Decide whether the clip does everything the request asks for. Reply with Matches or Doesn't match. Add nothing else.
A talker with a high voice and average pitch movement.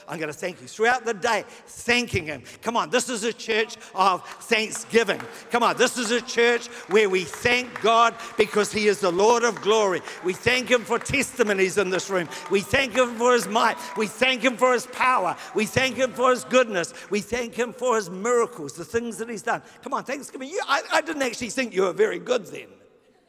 Matches